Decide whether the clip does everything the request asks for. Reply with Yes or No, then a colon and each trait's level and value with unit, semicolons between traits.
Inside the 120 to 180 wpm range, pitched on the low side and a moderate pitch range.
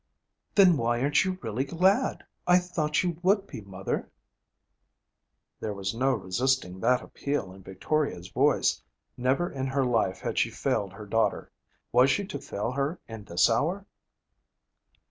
No: average, 150 wpm; low, 130 Hz; wide, 7.7 semitones